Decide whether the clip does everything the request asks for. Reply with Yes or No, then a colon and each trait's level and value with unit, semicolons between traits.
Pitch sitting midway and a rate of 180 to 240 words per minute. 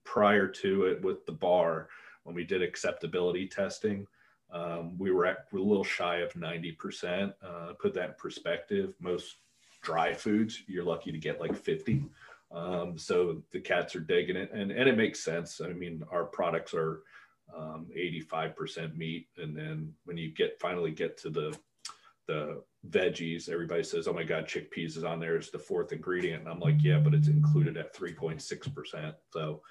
No: low, 100 Hz; average, 190 wpm